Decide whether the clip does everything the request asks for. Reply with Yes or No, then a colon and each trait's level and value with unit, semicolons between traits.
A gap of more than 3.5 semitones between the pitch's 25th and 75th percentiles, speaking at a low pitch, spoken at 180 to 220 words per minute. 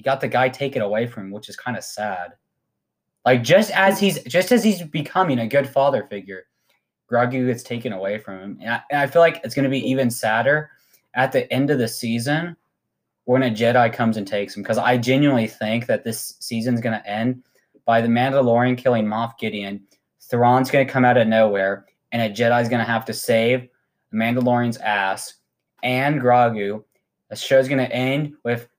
No: average, 3.2 semitones; low, 120 Hz; average, 190 wpm